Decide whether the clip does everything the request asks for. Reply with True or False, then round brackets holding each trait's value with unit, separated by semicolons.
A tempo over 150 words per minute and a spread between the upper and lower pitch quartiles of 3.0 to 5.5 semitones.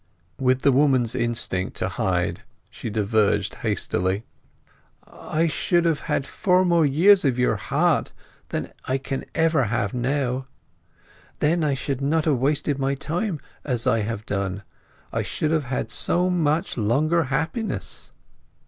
False (140 wpm; 5.0 semitones)